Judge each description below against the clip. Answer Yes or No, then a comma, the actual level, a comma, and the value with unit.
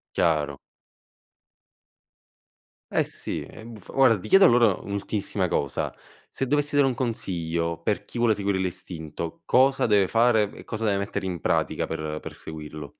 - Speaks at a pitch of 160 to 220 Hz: No, low, 100 Hz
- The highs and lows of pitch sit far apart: Yes, wide, 5.9 semitones